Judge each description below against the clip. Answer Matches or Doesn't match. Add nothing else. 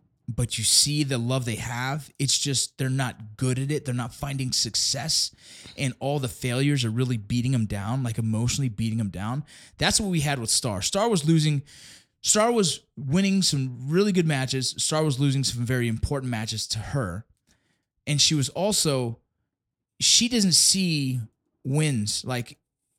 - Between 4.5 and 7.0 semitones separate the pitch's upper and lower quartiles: Doesn't match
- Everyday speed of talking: Matches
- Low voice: Matches